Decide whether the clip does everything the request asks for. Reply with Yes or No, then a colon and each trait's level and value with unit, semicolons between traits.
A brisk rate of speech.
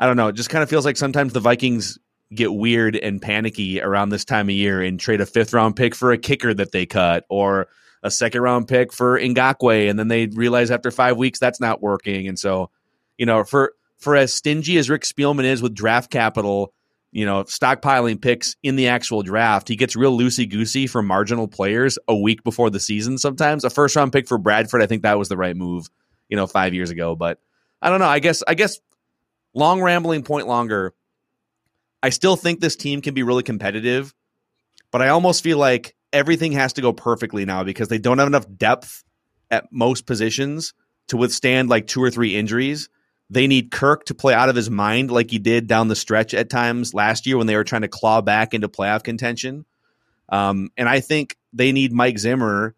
Yes: fast, 215 wpm